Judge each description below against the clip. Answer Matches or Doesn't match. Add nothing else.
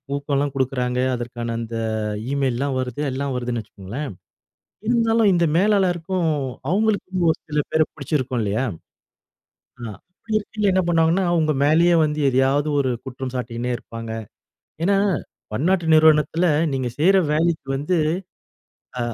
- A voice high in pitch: Doesn't match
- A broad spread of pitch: Matches